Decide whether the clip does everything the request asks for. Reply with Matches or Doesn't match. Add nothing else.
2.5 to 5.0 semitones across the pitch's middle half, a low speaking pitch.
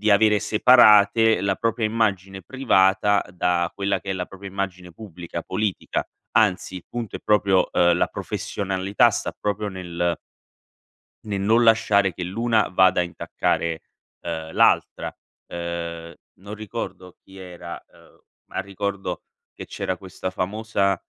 Matches